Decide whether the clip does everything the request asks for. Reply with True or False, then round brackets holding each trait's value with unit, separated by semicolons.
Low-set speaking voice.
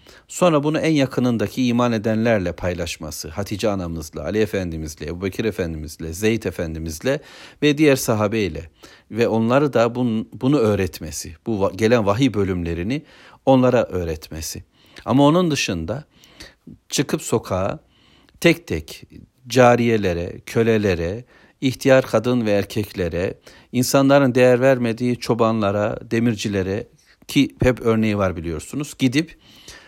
True (110 Hz)